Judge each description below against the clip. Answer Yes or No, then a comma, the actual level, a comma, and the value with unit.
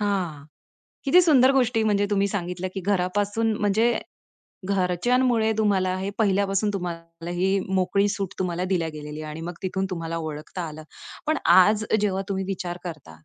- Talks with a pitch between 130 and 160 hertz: No, high, 190 Hz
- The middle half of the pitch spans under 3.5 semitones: Yes, average, 2.9 semitones